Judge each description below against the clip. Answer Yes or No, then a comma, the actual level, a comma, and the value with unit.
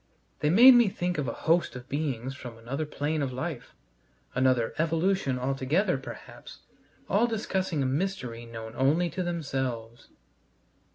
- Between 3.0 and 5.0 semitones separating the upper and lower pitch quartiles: No, wide, 5.6 semitones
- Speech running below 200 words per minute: Yes, average, 145 wpm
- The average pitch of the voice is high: No, medium, 140 Hz